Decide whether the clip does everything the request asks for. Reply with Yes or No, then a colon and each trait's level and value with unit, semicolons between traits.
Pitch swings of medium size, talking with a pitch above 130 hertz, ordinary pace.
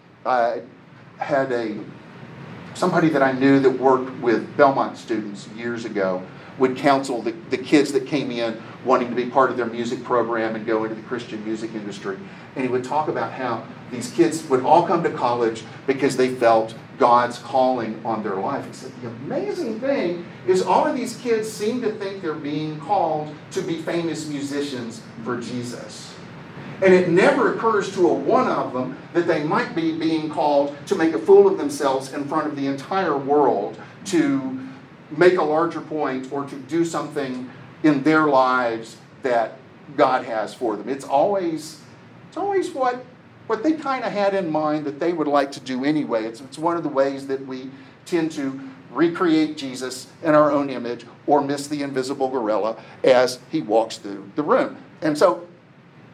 Yes: average, 5.0 semitones; medium, 140 Hz; average, 185 wpm